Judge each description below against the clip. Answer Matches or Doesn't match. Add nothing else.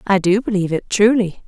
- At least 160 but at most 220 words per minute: Matches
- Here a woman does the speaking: Matches